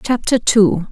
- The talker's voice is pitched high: Yes, high, 210 Hz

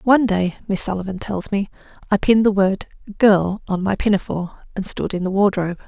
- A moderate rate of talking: Yes, average, 195 wpm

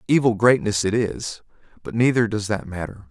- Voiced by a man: Yes, male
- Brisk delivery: No, average, 155 wpm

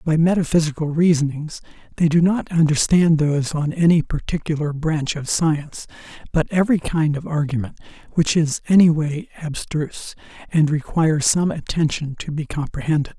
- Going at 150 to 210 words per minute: No, average, 140 wpm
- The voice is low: No, medium, 155 Hz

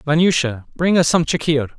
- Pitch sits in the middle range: Yes, medium, 155 Hz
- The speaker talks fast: No, average, 170 wpm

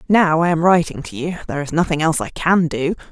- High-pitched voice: No, medium, 165 Hz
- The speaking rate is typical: No, fast, 250 wpm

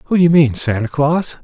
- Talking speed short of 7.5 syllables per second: Yes, 4.4 syllables/s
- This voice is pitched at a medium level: Yes, medium, 145 Hz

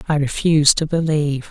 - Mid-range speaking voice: Yes, medium, 150 Hz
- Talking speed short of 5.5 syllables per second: No, 6.0 syllables/s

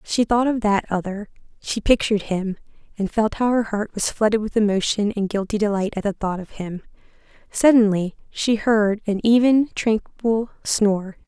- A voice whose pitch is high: Yes, high, 210 Hz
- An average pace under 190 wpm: Yes, average, 170 wpm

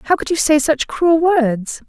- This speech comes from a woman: Yes, female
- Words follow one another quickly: Yes, fast, 225 wpm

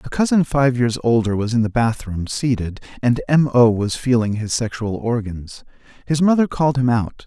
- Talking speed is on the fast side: No, average, 190 wpm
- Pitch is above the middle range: No, low, 120 Hz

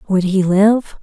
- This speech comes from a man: No, female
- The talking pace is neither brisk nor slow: Yes, average, 175 wpm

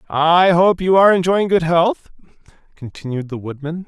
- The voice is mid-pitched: Yes, medium, 170 Hz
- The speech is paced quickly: No, average, 155 wpm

